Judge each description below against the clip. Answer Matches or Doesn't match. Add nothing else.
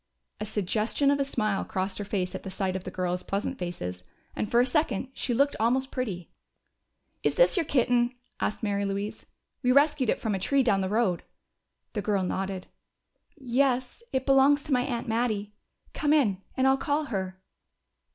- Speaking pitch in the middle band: Doesn't match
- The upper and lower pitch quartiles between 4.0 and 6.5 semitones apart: Matches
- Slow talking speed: Doesn't match